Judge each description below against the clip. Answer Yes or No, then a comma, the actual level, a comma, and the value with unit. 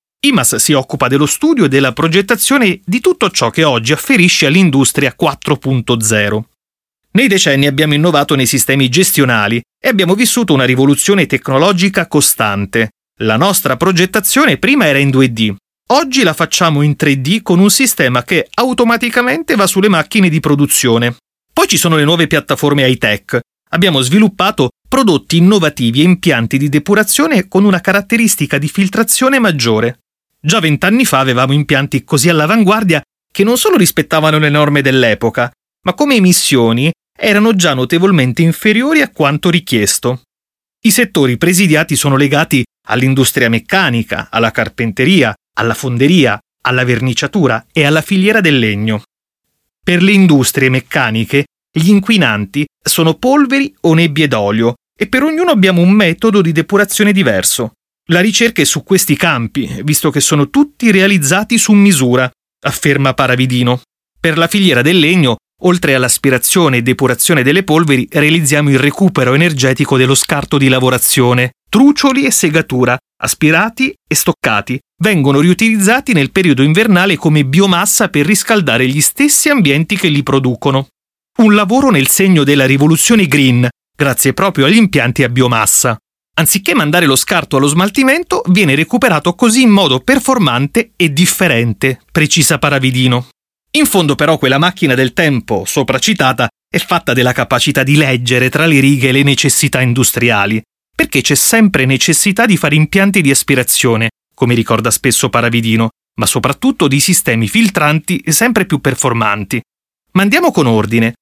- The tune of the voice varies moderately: No, wide, 6.7 semitones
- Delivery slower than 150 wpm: Yes, average, 140 wpm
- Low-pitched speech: No, medium, 150 Hz